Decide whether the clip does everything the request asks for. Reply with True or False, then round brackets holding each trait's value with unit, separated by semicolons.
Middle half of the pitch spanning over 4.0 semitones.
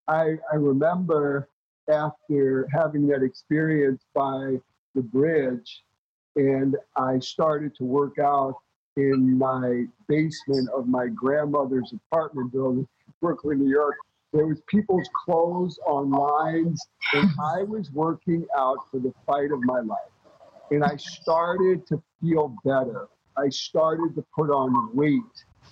False (3.2 semitones)